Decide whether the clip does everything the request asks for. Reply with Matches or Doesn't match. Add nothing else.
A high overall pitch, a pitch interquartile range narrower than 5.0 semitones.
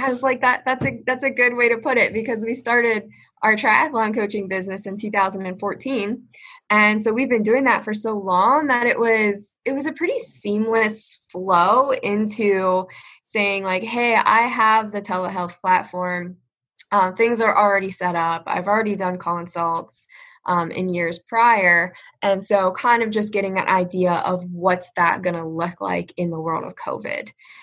Matches